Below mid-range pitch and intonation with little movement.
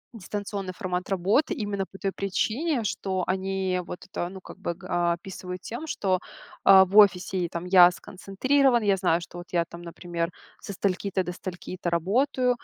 No: high, 190 Hz; narrow, 2.3 semitones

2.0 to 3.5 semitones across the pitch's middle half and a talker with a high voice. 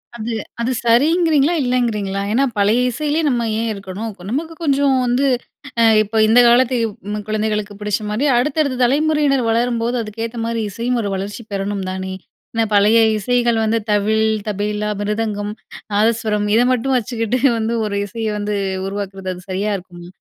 Yes: average, 3.1 semitones; high, 225 Hz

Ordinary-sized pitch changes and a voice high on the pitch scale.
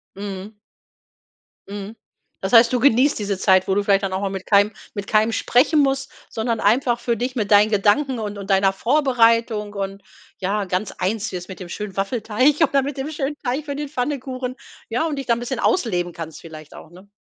Yes: average, 4.6 semitones; high, 215 Hz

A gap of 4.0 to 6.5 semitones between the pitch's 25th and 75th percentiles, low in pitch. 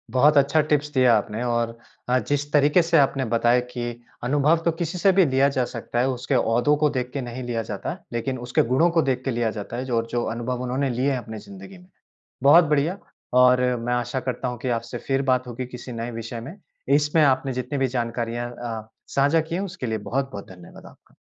No: average, 3.2 semitones; low, 130 Hz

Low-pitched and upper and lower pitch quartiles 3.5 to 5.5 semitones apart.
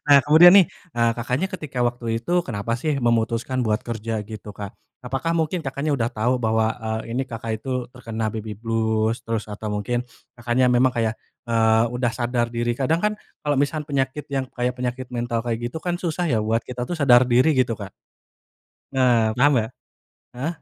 No: low, 120 Hz; average, 3.0 semitones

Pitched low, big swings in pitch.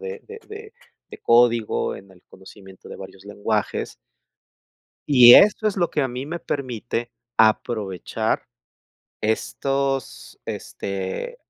Yes: low, 120 Hz; wide, 6.2 semitones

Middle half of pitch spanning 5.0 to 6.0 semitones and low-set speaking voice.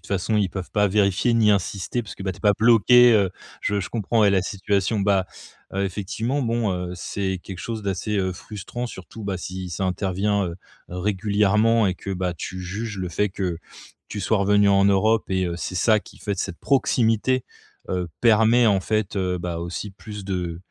No: narrow, 2.6 semitones; low, 100 Hz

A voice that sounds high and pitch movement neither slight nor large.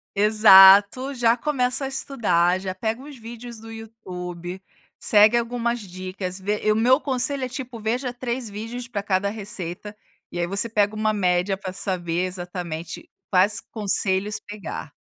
Yes: high, 210 Hz; average, 4.1 semitones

